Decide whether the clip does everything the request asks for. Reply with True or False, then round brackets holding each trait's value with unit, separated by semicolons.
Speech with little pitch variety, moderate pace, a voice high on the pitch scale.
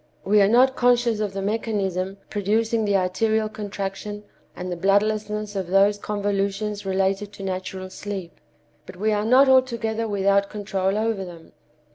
True (1.9 semitones; 150 wpm; 205 Hz)